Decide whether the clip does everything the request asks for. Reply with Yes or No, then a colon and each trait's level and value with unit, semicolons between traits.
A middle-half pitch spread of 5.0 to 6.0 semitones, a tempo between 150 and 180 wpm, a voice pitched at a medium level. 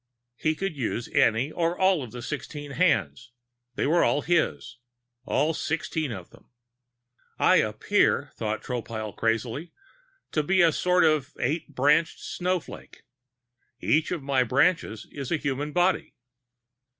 No: wide, 5.4 semitones; average, 140 wpm; medium, 145 Hz